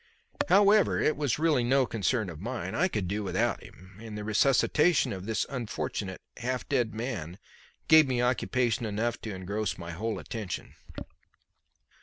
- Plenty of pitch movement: No, average, 4.3 semitones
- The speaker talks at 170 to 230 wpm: No, average, 155 wpm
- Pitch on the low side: Yes, low, 115 Hz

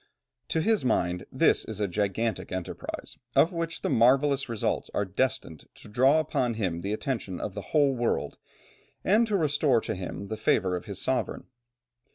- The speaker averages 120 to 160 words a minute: No, average, 175 wpm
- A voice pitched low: Yes, low, 115 Hz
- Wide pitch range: Yes, wide, 6.4 semitones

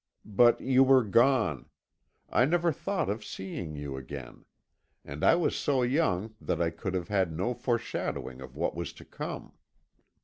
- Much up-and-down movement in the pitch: Yes, wide, 7.7 semitones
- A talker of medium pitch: No, low, 105 Hz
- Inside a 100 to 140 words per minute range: No, average, 165 wpm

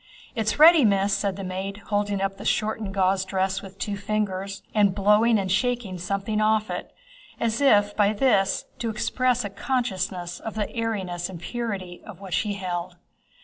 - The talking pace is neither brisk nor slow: Yes, average, 175 wpm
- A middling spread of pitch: No, narrow, 2.3 semitones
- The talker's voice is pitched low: No, high, 200 Hz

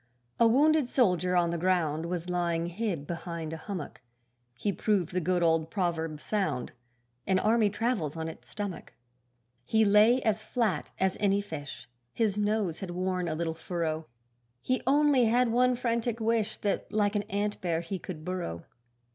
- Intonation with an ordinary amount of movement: Yes, average, 4.5 semitones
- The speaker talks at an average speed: Yes, average, 165 wpm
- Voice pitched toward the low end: No, medium, 185 Hz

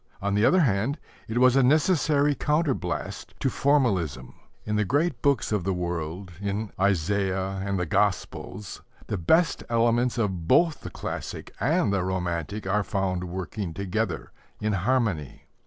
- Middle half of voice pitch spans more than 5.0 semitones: Yes, wide, 5.4 semitones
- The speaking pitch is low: Yes, low, 100 Hz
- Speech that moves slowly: No, average, 150 wpm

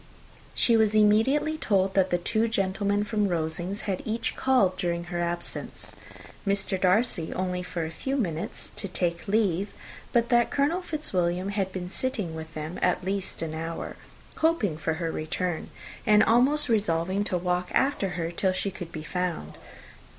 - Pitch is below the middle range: No, high, 190 Hz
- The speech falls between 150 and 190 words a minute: Yes, average, 165 wpm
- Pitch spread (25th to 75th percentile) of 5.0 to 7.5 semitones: No, average, 3.9 semitones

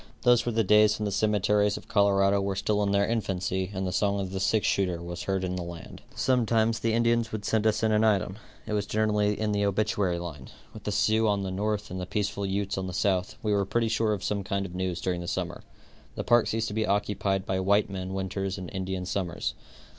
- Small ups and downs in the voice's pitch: Yes, narrow, 2.2 semitones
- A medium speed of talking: No, fast, 240 wpm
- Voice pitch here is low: Yes, low, 100 Hz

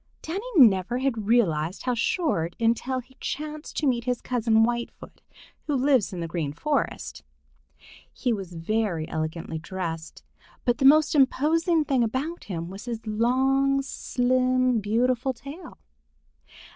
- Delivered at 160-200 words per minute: No, slow, 135 wpm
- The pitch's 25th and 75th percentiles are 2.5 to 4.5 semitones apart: No, average, 5.3 semitones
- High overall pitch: Yes, high, 245 Hz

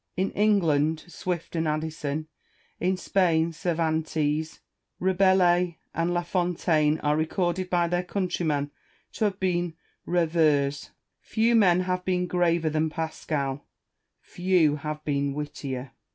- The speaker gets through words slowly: Yes, slow, 120 wpm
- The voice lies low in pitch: No, medium, 165 Hz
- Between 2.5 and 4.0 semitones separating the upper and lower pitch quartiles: Yes, average, 2.9 semitones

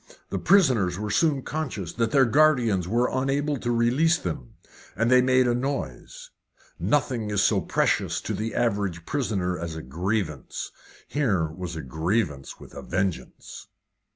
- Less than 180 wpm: Yes, average, 155 wpm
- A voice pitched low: Yes, low, 110 Hz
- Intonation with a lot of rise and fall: Yes, wide, 6.5 semitones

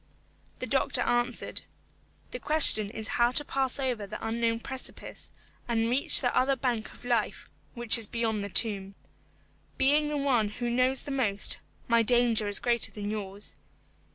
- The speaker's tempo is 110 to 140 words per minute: No, average, 160 wpm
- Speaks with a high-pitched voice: Yes, high, 235 Hz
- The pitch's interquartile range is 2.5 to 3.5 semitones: Yes, average, 2.9 semitones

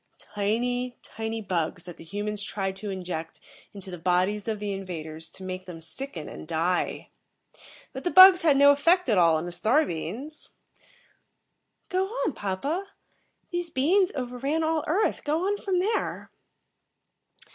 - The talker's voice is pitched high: Yes, high, 215 Hz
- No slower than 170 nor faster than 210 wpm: No, average, 155 wpm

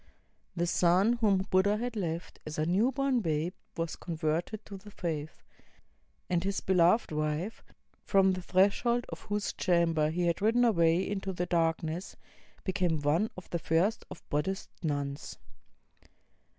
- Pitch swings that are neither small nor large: Yes, average, 3.7 semitones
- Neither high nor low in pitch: Yes, medium, 180 Hz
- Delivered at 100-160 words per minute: Yes, average, 150 wpm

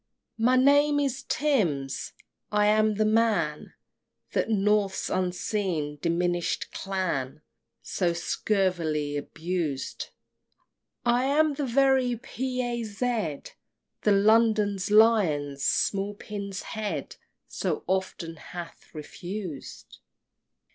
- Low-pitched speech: No, high, 205 Hz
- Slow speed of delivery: Yes, slow, 100 wpm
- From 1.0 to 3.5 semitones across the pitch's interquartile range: No, average, 5.2 semitones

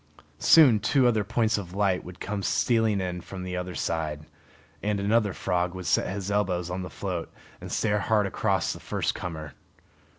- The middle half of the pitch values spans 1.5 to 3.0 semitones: Yes, average, 2.7 semitones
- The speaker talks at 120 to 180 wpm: No, average, 190 wpm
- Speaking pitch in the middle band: No, very low, 95 Hz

